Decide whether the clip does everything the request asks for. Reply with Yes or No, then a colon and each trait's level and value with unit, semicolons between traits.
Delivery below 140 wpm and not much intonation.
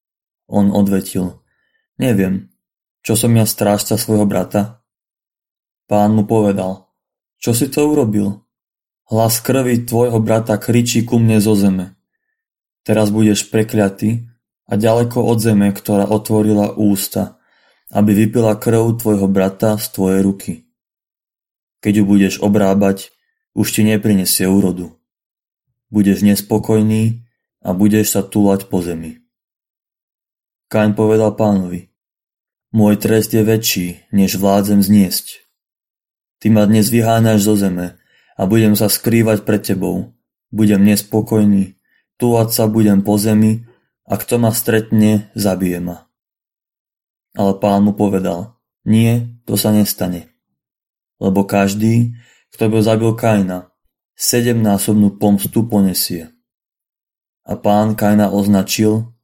Yes: average, 120 wpm; narrow, 2.1 semitones